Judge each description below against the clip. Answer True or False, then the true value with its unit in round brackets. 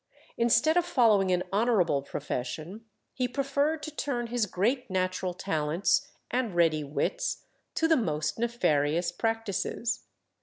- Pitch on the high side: True (220 Hz)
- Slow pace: True (125 wpm)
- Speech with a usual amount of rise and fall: False (6.4 semitones)